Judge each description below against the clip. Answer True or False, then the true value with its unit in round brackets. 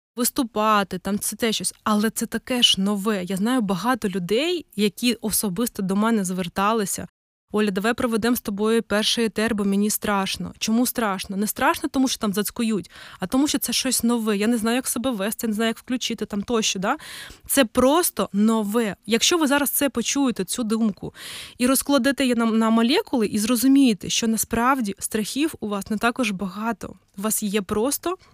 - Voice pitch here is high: True (225 Hz)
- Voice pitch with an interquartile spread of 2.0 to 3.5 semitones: True (3.2 semitones)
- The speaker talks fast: True (180 wpm)